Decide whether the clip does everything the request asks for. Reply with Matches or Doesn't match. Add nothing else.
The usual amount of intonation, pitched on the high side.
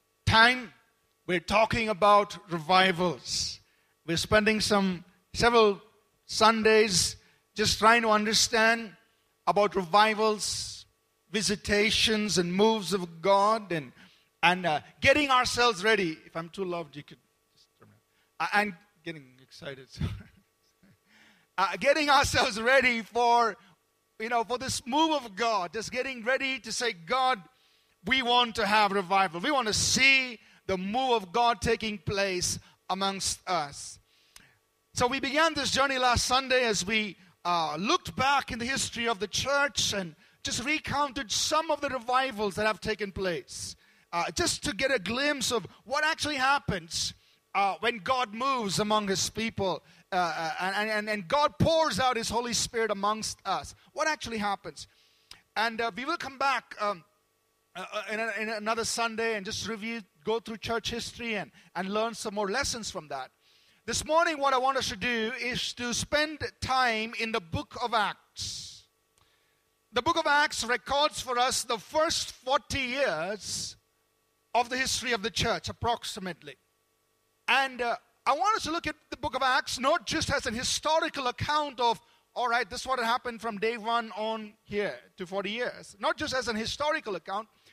Matches